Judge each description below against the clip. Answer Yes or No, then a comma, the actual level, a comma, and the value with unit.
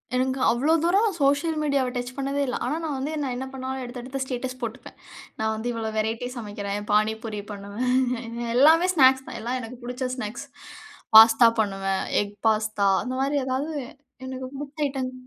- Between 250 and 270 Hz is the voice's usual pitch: Yes, very high, 255 Hz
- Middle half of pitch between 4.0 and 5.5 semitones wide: No, average, 3.4 semitones